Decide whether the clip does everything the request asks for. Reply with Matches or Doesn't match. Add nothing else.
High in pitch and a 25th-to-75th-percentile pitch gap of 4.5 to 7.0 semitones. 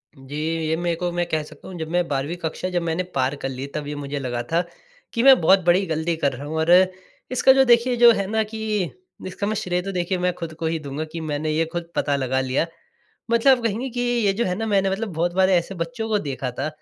Doesn't match